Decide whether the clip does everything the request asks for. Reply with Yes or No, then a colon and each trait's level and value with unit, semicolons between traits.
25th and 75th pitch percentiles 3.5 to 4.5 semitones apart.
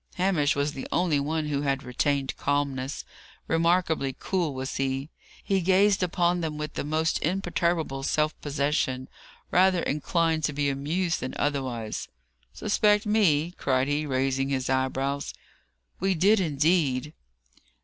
Yes: average, 4.1 semitones